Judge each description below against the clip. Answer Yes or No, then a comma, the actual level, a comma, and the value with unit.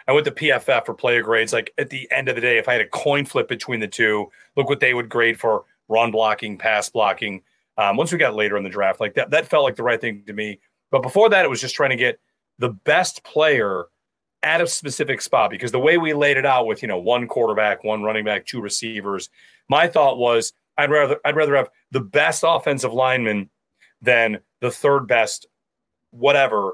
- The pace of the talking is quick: Yes, fast, 225 wpm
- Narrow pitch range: No, average, 4.0 semitones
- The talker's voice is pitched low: Yes, low, 115 Hz